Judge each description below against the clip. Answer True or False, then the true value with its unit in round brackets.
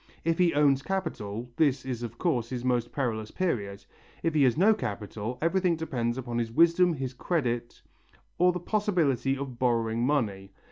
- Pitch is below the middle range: True (130 Hz)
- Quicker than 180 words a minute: False (170 wpm)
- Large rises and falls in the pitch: True (5.8 semitones)